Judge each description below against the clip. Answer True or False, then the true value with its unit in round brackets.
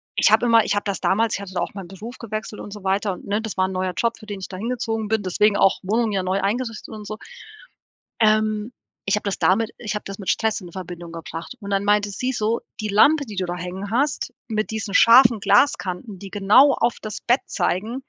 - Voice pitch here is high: True (210 Hz)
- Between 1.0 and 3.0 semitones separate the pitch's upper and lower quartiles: True (2.7 semitones)